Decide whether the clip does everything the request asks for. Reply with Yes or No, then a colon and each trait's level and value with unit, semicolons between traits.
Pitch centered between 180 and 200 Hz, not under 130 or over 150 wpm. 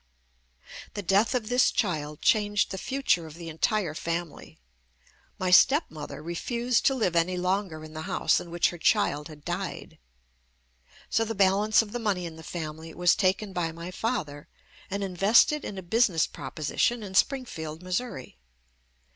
No: medium, 185 Hz; average, 165 wpm